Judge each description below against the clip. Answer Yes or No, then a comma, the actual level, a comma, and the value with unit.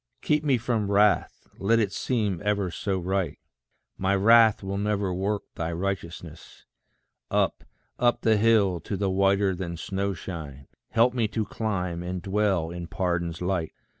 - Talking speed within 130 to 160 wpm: Yes, average, 155 wpm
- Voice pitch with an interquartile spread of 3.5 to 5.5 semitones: No, average, 3.1 semitones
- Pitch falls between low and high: No, very low, 95 Hz